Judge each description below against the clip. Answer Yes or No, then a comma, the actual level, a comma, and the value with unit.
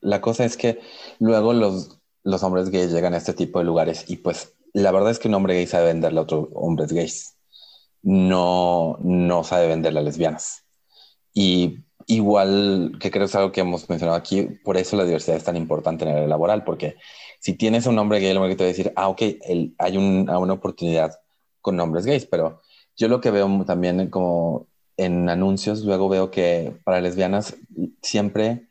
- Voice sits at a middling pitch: No, very low, 95 Hz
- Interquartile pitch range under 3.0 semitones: Yes, narrow, 2.6 semitones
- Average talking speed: No, fast, 205 wpm